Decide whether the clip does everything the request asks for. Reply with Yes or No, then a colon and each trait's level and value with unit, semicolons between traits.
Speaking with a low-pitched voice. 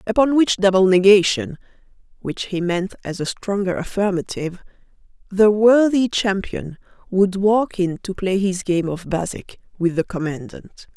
No: high, 190 Hz